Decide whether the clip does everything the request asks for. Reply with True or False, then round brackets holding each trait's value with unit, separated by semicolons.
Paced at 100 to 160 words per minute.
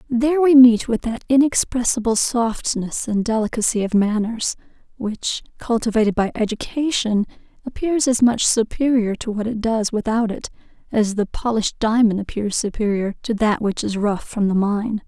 True (155 wpm)